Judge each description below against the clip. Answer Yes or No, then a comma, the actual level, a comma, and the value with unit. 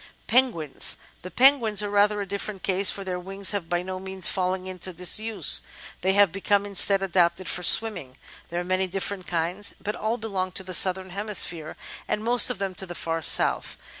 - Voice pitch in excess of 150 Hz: Yes, high, 190 Hz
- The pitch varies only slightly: Yes, narrow, 2.2 semitones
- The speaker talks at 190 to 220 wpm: Yes, average, 195 wpm